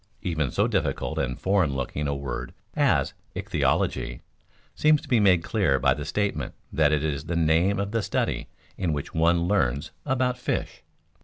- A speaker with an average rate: Yes, average, 170 wpm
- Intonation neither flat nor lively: No, wide, 5.8 semitones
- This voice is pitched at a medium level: No, very low, 85 Hz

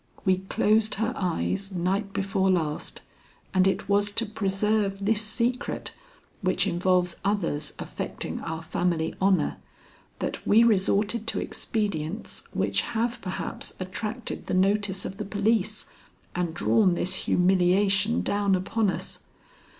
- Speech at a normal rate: No, slow, 125 wpm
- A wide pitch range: No, narrow, 2.5 semitones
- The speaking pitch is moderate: No, high, 195 Hz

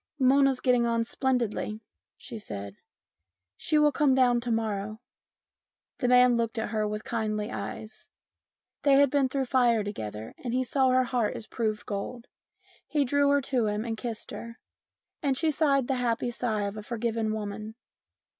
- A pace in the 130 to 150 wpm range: No, average, 180 wpm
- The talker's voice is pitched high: Yes, high, 235 Hz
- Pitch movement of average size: Yes, average, 3.4 semitones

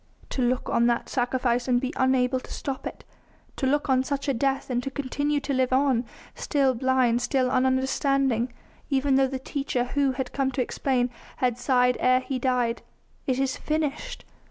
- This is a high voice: Yes, very high, 260 Hz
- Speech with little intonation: Yes, narrow, 1.6 semitones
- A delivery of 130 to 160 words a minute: No, average, 180 wpm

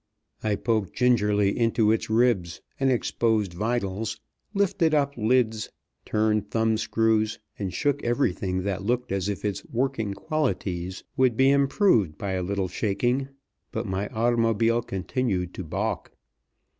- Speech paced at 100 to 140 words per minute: Yes, slow, 135 wpm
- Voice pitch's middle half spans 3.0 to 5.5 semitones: Yes, average, 3.8 semitones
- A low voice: Yes, low, 110 Hz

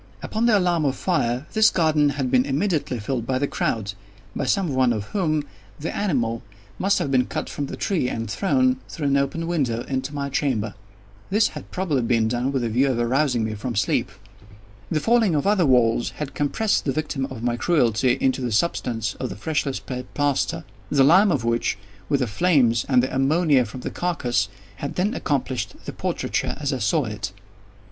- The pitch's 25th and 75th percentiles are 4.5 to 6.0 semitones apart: Yes, average, 4.8 semitones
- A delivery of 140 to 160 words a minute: No, average, 195 wpm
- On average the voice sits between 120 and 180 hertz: Yes, low, 135 Hz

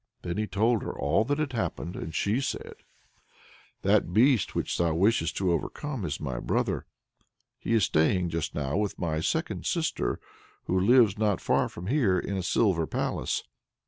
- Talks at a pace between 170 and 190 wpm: Yes, average, 175 wpm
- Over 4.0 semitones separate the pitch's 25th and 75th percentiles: Yes, average, 5.2 semitones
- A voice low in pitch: Yes, very low, 95 Hz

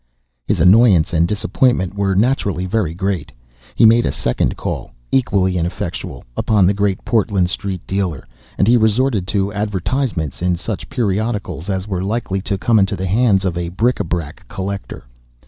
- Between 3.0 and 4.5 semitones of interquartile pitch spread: Yes, average, 3.3 semitones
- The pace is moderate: Yes, average, 165 wpm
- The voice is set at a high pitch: No, low, 100 Hz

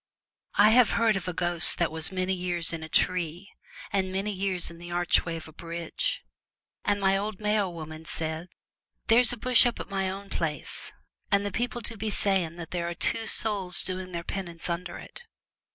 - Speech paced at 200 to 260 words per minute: Yes, fast, 205 wpm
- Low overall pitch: No, medium, 185 Hz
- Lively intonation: No, average, 3.0 semitones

